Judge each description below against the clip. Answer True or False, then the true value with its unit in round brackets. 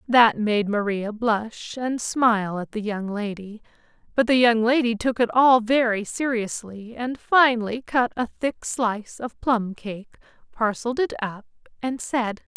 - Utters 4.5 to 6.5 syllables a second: False (4.3 syllables/s)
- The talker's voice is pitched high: True (230 Hz)